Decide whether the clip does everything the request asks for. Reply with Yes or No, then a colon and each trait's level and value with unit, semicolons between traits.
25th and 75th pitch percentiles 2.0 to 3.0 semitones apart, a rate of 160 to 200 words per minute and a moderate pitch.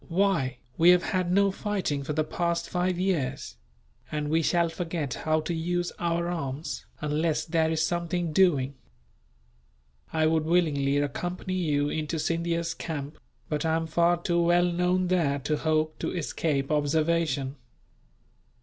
No: narrow, 2.5 semitones; average, 150 wpm; medium, 165 Hz